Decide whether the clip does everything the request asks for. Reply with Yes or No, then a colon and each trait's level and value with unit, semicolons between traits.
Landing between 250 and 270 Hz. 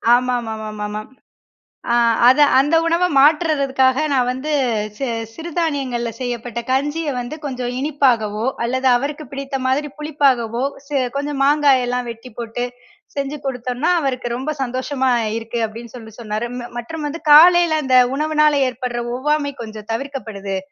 Yes: very high, 260 Hz